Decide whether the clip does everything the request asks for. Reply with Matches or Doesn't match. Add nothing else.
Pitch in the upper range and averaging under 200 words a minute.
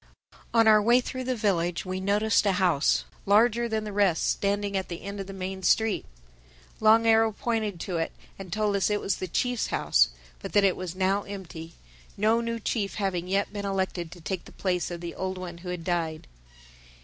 Doesn't match